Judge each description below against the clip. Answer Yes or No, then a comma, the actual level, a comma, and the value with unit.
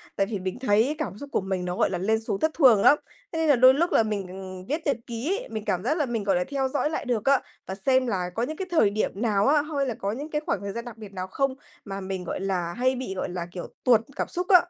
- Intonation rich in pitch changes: Yes, wide, 6.3 semitones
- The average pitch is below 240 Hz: Yes, high, 225 Hz